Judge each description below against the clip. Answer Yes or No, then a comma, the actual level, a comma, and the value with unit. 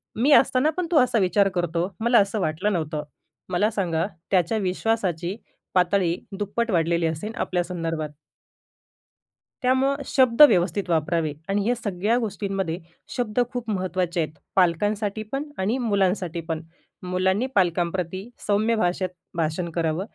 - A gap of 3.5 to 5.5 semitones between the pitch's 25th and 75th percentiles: Yes, average, 4.1 semitones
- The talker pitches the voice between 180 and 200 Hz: Yes, high, 190 Hz